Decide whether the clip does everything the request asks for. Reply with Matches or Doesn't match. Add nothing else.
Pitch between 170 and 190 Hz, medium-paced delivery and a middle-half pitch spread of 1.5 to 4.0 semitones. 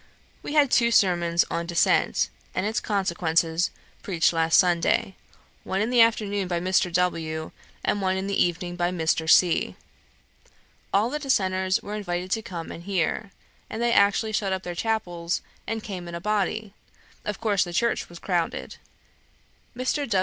Matches